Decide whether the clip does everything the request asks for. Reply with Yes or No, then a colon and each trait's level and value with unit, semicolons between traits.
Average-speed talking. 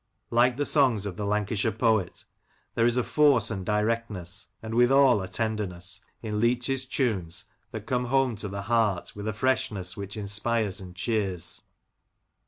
Yes: average, 160 wpm